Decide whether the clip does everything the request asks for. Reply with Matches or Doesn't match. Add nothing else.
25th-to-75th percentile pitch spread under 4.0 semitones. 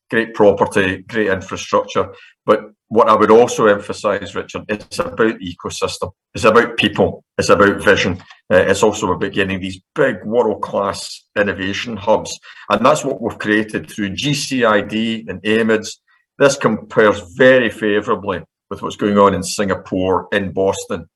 Matches